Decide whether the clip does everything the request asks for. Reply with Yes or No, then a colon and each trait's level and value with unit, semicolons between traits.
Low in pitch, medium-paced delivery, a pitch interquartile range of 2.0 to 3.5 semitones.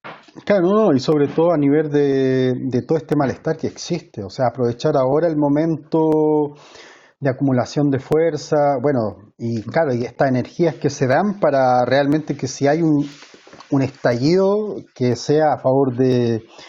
No: medium, 145 Hz; average, 165 wpm; average, 3.2 semitones